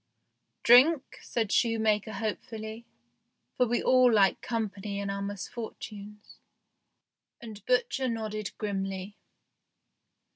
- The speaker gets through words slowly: Yes, slow, 105 wpm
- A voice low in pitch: No, high, 215 Hz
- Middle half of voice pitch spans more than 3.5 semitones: No, narrow, 2.6 semitones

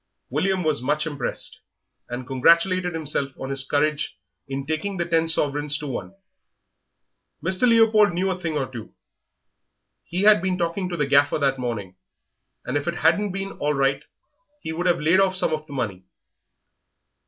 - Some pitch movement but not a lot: Yes, average, 4.9 semitones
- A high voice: No, medium, 155 Hz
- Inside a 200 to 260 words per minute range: No, average, 175 wpm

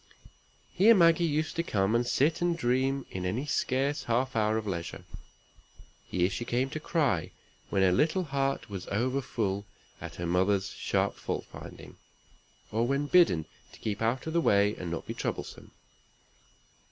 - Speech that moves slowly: No, average, 165 wpm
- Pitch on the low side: Yes, low, 120 Hz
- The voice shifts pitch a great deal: Yes, wide, 6.6 semitones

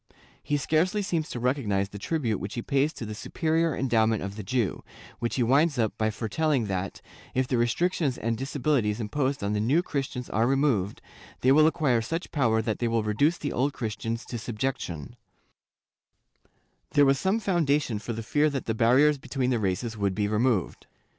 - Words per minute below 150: No, average, 185 wpm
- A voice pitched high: No, low, 125 Hz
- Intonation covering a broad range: No, average, 4.9 semitones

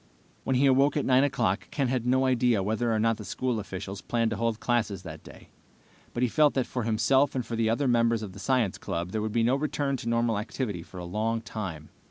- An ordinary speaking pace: No, fast, 240 wpm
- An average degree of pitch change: Yes, average, 3.4 semitones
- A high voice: No, low, 115 Hz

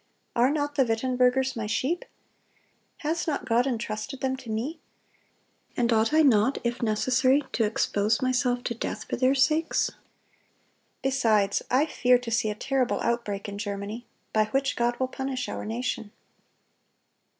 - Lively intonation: No, average, 3.2 semitones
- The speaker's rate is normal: Yes, average, 150 wpm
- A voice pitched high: Yes, high, 245 Hz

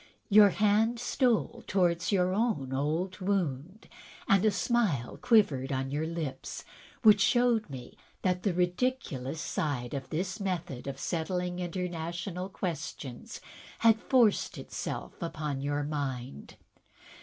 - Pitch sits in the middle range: Yes, medium, 180 Hz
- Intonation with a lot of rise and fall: Yes, wide, 5.9 semitones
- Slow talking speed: Yes, slow, 120 wpm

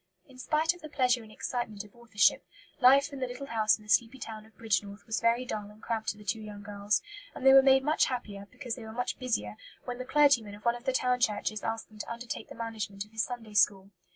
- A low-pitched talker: No, high, 230 Hz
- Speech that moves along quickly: Yes, fast, 255 wpm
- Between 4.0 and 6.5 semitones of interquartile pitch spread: No, average, 3.2 semitones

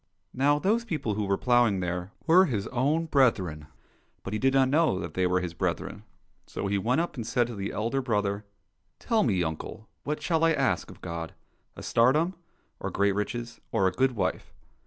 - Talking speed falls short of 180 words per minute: No, average, 200 wpm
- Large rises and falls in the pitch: Yes, wide, 6.1 semitones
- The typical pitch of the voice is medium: No, low, 110 Hz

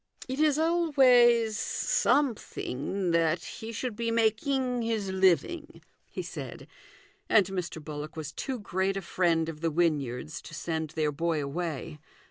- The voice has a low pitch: No, high, 190 Hz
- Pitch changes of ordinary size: No, wide, 6.9 semitones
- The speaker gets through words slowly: No, average, 145 wpm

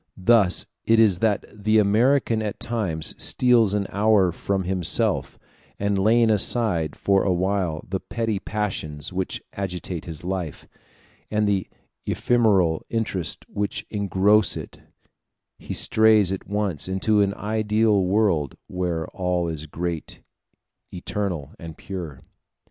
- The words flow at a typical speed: No, slow, 125 wpm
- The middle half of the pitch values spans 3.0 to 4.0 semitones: Yes, average, 3.3 semitones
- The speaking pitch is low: Yes, low, 100 Hz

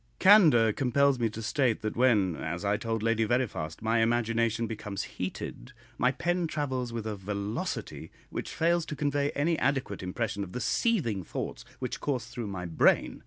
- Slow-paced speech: No, average, 170 wpm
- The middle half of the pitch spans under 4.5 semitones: No, average, 4.9 semitones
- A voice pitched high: No, low, 115 Hz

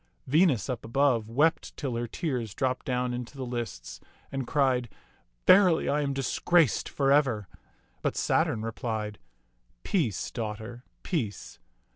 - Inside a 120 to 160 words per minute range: Yes, slow, 135 wpm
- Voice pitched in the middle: No, low, 125 Hz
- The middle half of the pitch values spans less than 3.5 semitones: No, average, 3.8 semitones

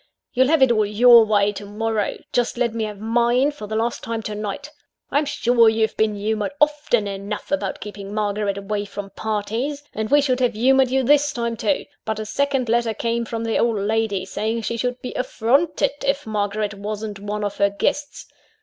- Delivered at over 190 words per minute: Yes, average, 200 wpm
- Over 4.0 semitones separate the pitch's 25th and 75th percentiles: No, average, 3.2 semitones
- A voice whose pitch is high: Yes, high, 225 Hz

